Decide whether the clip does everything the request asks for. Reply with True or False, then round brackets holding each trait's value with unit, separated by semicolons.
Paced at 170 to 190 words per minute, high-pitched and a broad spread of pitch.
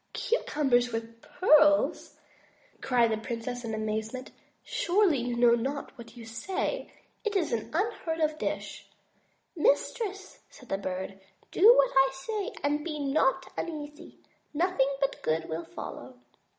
False (140 wpm; 270 Hz; 6.1 semitones)